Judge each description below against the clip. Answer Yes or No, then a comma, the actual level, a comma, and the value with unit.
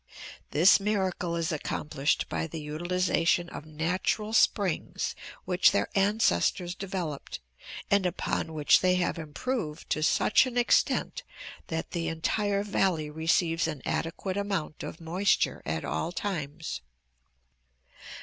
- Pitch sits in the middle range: Yes, medium, 175 Hz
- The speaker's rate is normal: No, slow, 120 wpm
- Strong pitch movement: No, average, 3.6 semitones